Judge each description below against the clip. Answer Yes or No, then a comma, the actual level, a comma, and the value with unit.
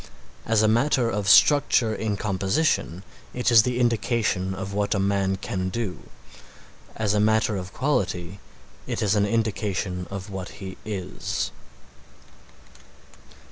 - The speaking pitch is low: Yes, low, 105 Hz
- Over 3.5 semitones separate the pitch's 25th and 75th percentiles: No, average, 3.0 semitones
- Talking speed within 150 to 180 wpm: No, slow, 135 wpm